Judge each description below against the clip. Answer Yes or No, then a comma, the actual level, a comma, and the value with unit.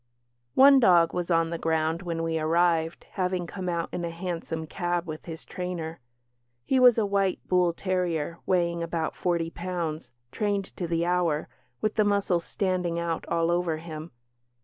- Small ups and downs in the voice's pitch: Yes, narrow, 1.7 semitones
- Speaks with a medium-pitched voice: Yes, medium, 170 Hz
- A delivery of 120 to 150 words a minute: No, average, 170 wpm